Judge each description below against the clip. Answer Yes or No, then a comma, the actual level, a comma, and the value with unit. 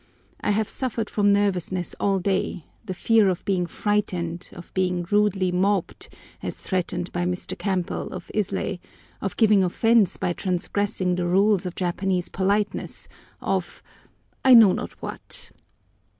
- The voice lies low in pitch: No, high, 190 Hz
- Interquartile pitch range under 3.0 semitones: Yes, narrow, 2.5 semitones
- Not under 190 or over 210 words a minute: No, slow, 135 wpm